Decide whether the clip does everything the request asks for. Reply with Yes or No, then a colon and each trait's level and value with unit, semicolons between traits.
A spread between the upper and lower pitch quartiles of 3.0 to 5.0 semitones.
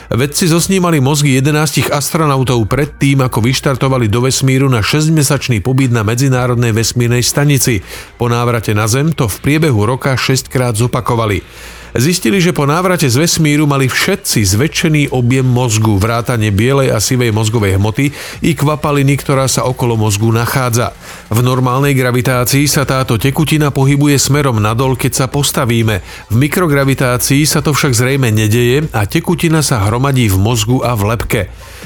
Yes: average, 3.5 semitones